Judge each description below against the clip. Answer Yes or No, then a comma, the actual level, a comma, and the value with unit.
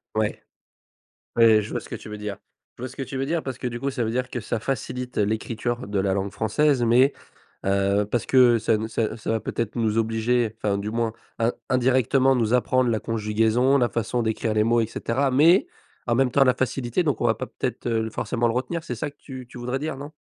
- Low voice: Yes, low, 120 Hz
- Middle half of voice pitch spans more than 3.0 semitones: No, average, 2.7 semitones